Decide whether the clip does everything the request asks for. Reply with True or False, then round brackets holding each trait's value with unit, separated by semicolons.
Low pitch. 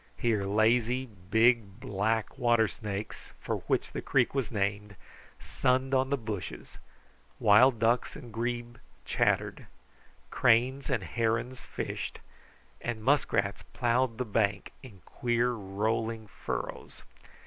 True (115 Hz)